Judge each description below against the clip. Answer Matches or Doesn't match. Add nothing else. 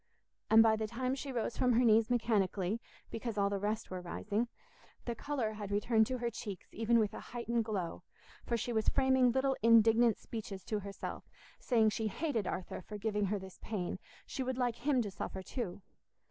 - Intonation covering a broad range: Doesn't match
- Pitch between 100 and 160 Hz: Doesn't match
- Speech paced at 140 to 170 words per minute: Doesn't match